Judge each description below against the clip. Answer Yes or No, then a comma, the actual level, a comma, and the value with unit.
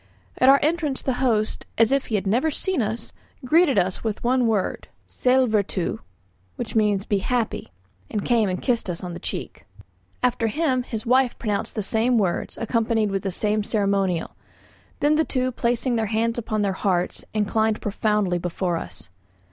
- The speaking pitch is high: Yes, high, 220 Hz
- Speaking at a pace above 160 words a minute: Yes, average, 170 wpm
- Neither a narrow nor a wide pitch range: Yes, average, 3.8 semitones